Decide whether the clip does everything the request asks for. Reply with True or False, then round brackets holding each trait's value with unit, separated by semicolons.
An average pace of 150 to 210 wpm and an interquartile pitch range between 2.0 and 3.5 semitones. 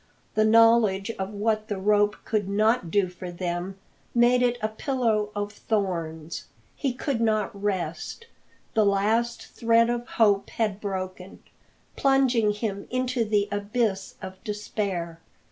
False (135 wpm; 2.9 semitones)